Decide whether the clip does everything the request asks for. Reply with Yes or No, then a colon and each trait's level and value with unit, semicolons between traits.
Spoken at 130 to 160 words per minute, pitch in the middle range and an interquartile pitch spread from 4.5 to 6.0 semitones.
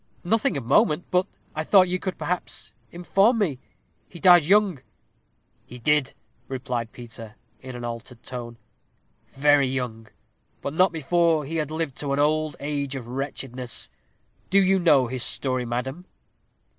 Yes: average, 150 wpm; medium, 145 Hz; wide, 5.4 semitones